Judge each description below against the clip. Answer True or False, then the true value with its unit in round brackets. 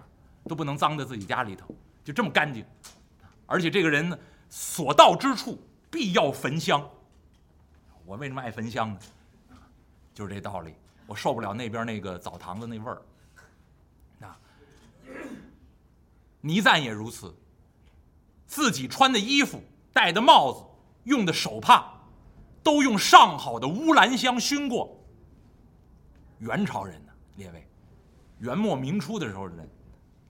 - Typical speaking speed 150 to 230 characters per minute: True (200 characters per minute)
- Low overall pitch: True (110 Hz)